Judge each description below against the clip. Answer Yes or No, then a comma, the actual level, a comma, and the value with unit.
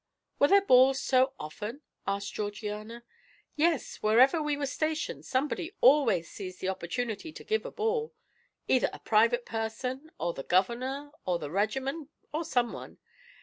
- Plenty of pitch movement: Yes, wide, 5.8 semitones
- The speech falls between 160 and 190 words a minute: No, average, 145 wpm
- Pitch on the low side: No, very high, 250 Hz